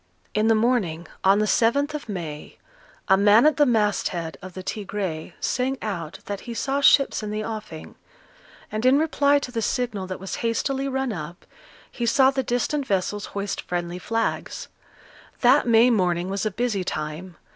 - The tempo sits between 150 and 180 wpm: Yes, average, 175 wpm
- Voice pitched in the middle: No, high, 215 Hz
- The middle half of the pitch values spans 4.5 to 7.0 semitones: Yes, average, 5.1 semitones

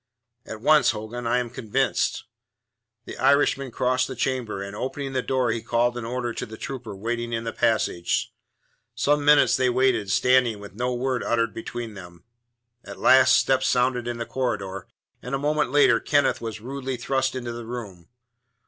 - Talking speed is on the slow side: No, average, 175 wpm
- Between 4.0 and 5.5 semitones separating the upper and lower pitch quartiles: No, narrow, 2.5 semitones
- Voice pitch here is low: Yes, low, 120 Hz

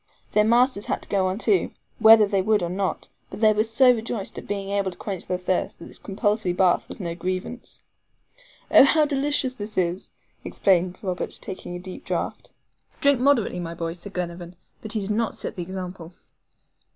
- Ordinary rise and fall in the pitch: Yes, average, 3.6 semitones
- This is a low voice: No, high, 195 Hz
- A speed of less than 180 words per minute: No, average, 195 wpm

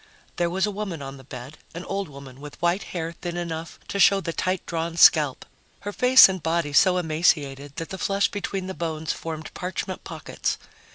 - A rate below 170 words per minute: No, average, 195 wpm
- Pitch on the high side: No, medium, 170 Hz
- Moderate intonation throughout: Yes, average, 3.5 semitones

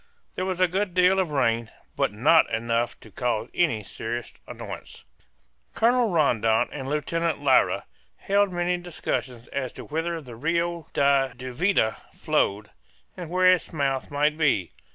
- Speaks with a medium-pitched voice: Yes, medium, 150 Hz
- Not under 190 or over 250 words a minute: No, average, 150 wpm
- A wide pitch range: Yes, wide, 6.5 semitones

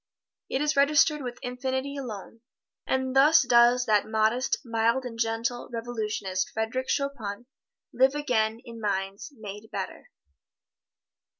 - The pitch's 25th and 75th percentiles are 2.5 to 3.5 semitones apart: Yes, average, 3.1 semitones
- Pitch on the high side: Yes, high, 240 Hz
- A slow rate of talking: Yes, slow, 120 wpm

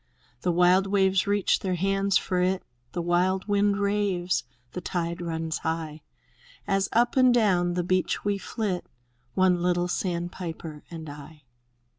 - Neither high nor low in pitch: Yes, medium, 180 Hz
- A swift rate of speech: No, average, 150 wpm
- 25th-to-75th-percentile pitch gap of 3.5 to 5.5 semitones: No, narrow, 2.4 semitones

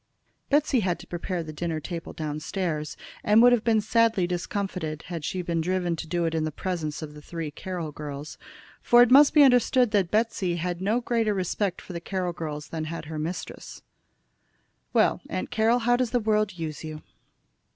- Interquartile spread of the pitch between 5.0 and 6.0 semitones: Yes, wide, 5.4 semitones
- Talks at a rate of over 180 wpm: Yes, average, 190 wpm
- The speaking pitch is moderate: Yes, medium, 180 Hz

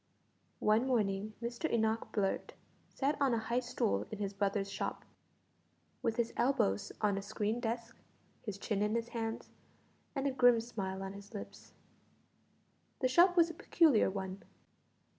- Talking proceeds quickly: No, average, 155 wpm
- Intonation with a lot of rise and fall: No, average, 3.4 semitones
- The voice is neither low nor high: No, high, 225 Hz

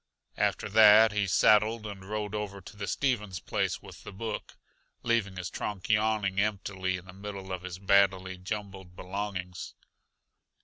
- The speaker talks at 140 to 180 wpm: Yes, average, 150 wpm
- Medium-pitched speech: No, low, 100 Hz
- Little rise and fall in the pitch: Yes, narrow, 2.0 semitones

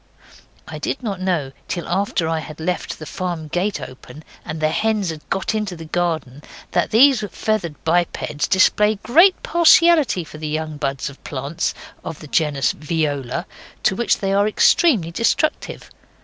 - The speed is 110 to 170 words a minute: Yes, average, 165 wpm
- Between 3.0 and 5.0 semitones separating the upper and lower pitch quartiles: No, wide, 5.4 semitones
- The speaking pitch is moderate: Yes, medium, 175 Hz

